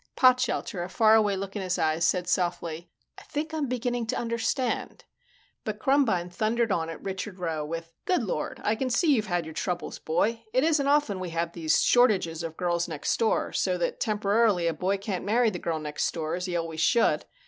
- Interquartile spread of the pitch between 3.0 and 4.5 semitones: No, wide, 5.5 semitones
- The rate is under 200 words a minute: No, fast, 205 wpm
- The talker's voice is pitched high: Yes, high, 195 Hz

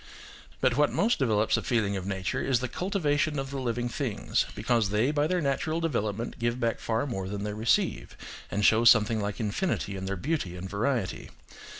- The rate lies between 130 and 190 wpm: No, average, 200 wpm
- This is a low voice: Yes, low, 115 Hz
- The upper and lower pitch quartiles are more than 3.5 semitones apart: Yes, average, 5.2 semitones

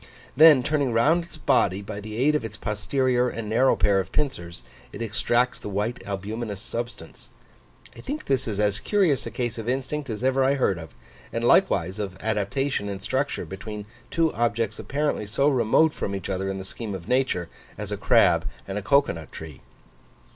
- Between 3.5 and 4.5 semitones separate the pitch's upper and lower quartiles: No, average, 4.9 semitones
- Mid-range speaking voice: No, low, 115 Hz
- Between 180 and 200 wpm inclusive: Yes, average, 190 wpm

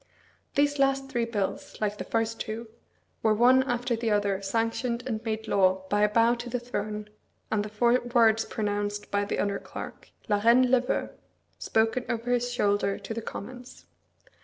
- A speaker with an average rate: Yes, average, 180 wpm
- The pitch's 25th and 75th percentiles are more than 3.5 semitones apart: No, average, 2.9 semitones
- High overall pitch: Yes, high, 225 Hz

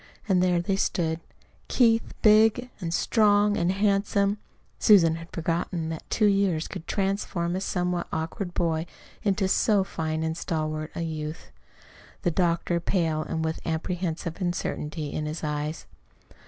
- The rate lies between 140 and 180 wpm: Yes, average, 145 wpm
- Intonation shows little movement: No, average, 3.5 semitones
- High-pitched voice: No, medium, 175 Hz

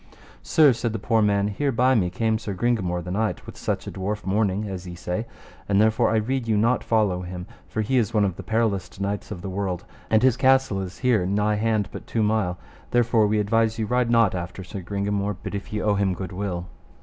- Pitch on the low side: Yes, low, 105 Hz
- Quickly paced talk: Yes, fast, 235 wpm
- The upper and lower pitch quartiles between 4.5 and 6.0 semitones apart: No, average, 2.9 semitones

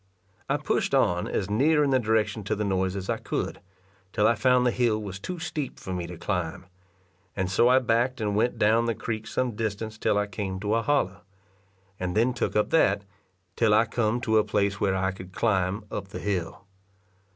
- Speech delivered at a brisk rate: Yes, fast, 210 wpm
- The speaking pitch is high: No, low, 105 Hz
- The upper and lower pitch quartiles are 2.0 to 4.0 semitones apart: Yes, average, 3.5 semitones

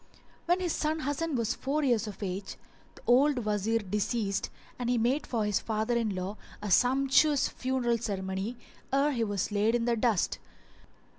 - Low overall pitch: No, high, 235 Hz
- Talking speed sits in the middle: Yes, average, 170 wpm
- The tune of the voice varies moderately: Yes, average, 4.2 semitones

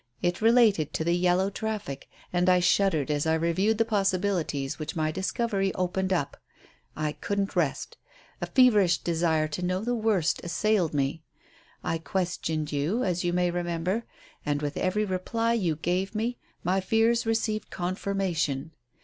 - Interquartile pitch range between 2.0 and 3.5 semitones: No, average, 4.1 semitones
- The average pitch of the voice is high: No, medium, 180 Hz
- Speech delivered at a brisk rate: No, average, 155 wpm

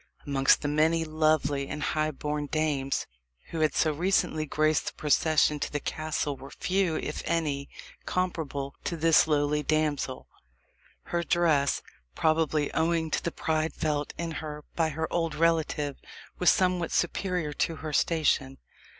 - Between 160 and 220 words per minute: No, average, 150 wpm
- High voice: No, medium, 155 Hz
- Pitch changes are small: Yes, narrow, 1.9 semitones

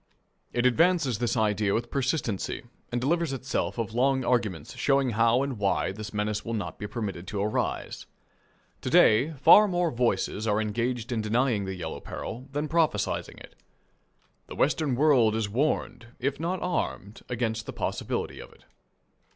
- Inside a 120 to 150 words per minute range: No, average, 165 wpm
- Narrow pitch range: No, average, 4.3 semitones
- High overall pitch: No, low, 120 Hz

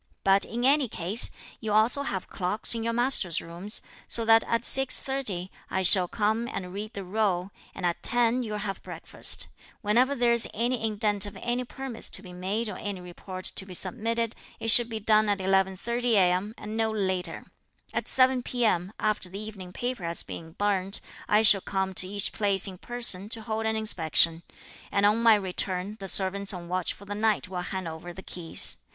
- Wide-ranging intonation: No, average, 3.5 semitones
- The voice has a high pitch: Yes, high, 205 Hz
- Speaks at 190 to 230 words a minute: Yes, average, 195 wpm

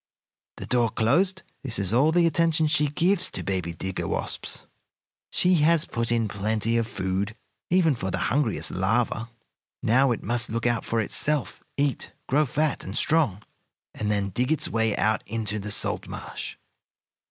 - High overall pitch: No, low, 115 Hz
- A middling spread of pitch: No, wide, 6.1 semitones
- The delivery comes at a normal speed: Yes, average, 165 wpm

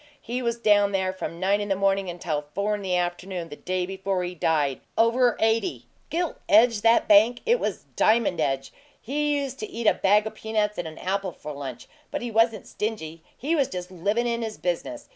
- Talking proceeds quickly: Yes, fast, 210 wpm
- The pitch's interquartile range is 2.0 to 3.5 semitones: No, average, 4.5 semitones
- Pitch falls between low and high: No, high, 205 Hz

